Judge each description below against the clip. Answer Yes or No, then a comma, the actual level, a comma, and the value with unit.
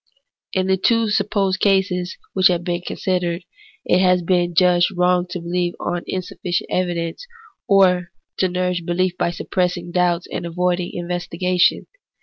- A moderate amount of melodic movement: No, narrow, 1.0 semitones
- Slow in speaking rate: No, average, 145 wpm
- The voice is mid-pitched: Yes, medium, 180 Hz